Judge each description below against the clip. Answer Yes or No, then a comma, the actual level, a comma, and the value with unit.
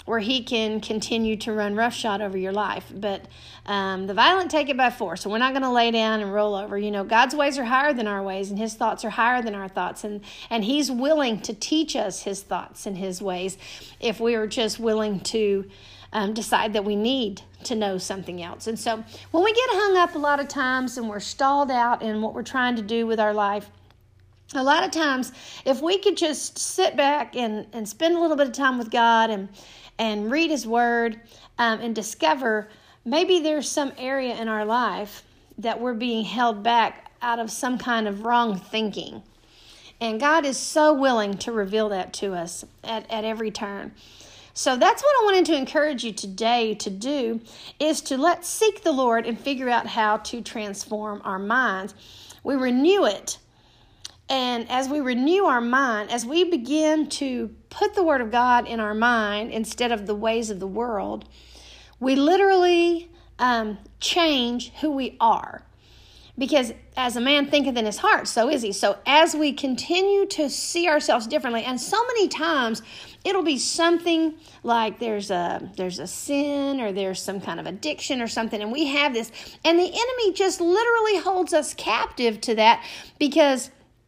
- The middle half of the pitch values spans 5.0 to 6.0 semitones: Yes, wide, 5.4 semitones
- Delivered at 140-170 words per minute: No, average, 195 wpm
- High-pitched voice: Yes, high, 235 Hz